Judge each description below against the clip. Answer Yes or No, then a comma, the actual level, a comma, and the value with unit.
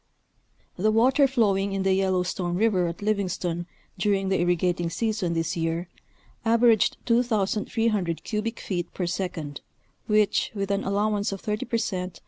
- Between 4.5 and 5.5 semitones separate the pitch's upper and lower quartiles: No, average, 3.4 semitones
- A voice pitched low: No, high, 195 Hz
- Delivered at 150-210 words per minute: No, average, 140 wpm